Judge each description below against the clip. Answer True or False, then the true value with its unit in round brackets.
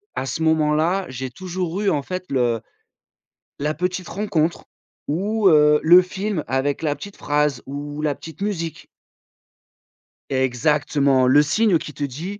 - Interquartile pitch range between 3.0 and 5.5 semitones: True (4.3 semitones)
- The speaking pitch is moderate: True (155 Hz)